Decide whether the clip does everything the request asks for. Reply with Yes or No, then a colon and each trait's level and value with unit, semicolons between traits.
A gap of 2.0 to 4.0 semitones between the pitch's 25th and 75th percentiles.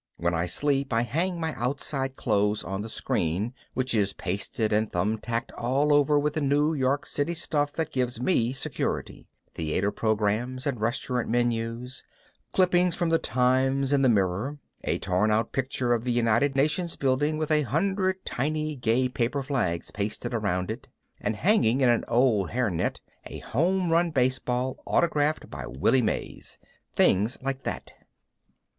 No: average, 4.9 semitones